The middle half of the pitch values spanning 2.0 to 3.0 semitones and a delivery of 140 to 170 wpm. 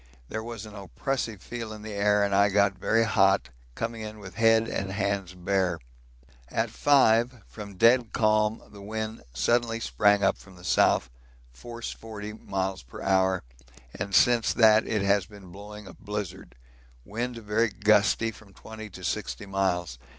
Yes: narrow, 2.4 semitones; average, 165 wpm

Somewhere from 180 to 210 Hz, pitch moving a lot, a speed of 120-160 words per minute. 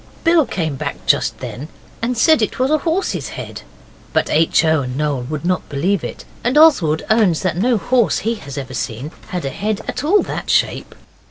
No: medium, 185 Hz; wide, 8.8 semitones; average, 200 wpm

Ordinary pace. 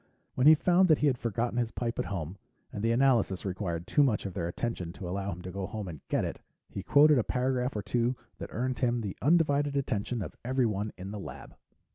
No: fast, 230 wpm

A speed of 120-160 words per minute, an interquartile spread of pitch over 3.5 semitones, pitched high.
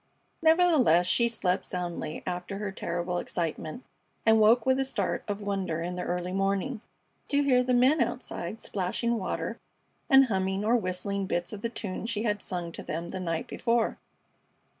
No: average, 170 wpm; average, 4.8 semitones; high, 200 Hz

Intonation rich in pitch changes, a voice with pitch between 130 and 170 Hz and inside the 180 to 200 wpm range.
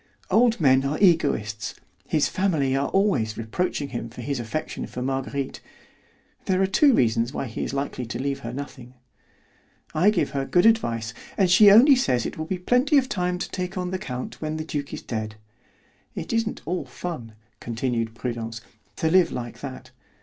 Yes: wide, 7.2 semitones; medium, 140 Hz; average, 185 wpm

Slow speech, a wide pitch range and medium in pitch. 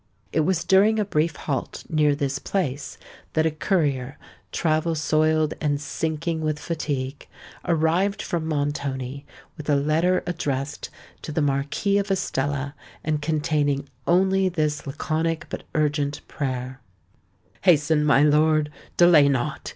No: slow, 130 wpm; narrow, 2.5 semitones; medium, 155 Hz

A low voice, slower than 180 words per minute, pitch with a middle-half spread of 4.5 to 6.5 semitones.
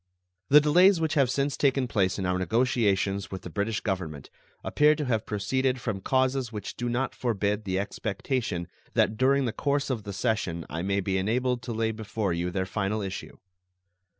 No: low, 110 Hz; average, 185 wpm; average, 5.0 semitones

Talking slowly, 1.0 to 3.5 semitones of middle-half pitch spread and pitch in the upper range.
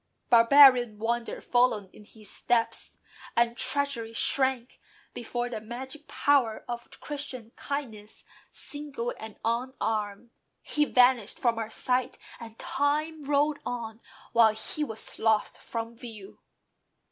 Yes: slow, 120 wpm; average, 3.0 semitones; high, 240 Hz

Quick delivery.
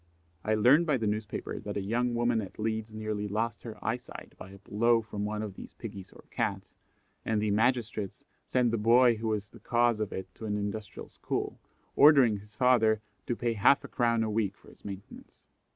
Yes: fast, 210 wpm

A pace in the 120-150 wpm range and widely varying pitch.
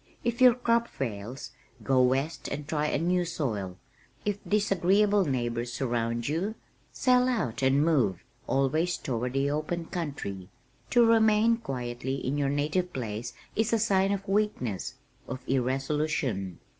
Yes: average, 140 wpm; wide, 7.8 semitones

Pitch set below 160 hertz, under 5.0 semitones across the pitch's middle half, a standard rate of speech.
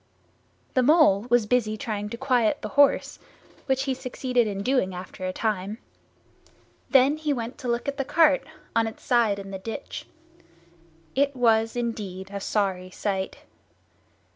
No: high, 230 Hz; average, 4.5 semitones; average, 155 wpm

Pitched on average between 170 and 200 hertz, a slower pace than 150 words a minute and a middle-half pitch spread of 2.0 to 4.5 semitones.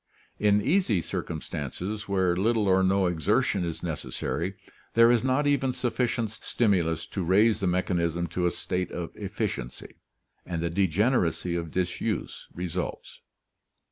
No: very low, 95 Hz; slow, 135 wpm; average, 4.1 semitones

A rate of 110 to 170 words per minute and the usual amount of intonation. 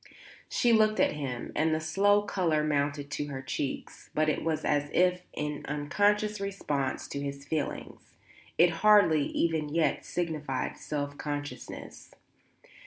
Yes: average, 140 wpm; average, 3.9 semitones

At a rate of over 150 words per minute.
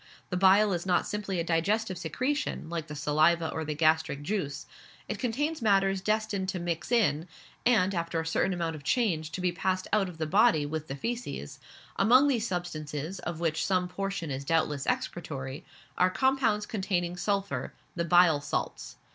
Yes: average, 175 wpm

